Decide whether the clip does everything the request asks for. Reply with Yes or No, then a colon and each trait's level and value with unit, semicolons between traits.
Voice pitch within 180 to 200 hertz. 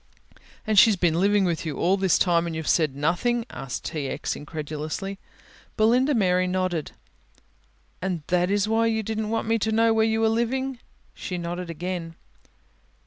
Yes: medium, 185 Hz